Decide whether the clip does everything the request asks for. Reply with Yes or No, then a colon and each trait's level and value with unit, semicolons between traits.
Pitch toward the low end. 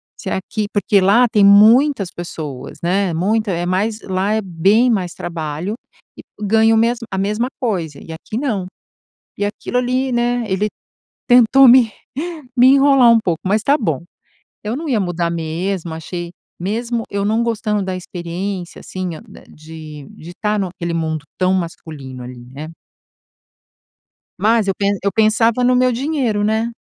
No: high, 200 Hz